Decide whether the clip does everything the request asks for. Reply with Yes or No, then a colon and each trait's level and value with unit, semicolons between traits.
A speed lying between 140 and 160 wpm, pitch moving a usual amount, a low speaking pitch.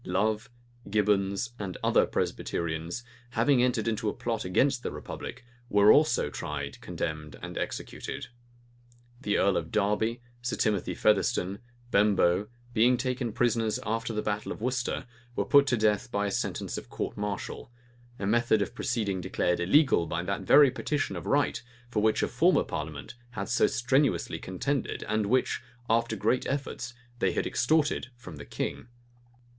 Yes: average, 155 wpm; average, 3.9 semitones; low, 110 Hz